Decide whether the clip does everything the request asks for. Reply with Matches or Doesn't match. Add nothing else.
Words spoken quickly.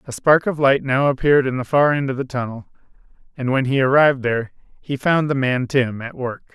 Matches